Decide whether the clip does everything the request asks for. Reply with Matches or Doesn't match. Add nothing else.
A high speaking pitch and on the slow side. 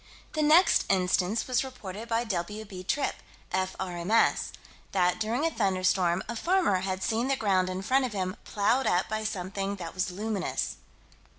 Doesn't match